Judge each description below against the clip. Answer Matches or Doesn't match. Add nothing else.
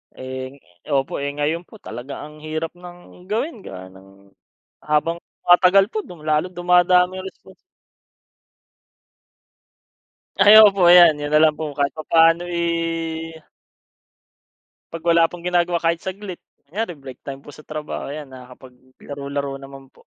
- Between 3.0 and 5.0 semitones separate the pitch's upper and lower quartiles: Matches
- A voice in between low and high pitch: Matches